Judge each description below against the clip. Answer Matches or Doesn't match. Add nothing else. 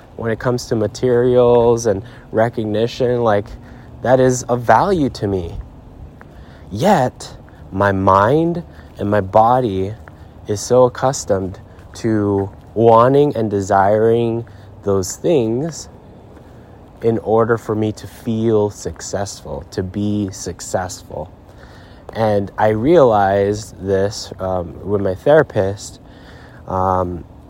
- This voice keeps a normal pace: Doesn't match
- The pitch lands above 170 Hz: Doesn't match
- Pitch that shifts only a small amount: Doesn't match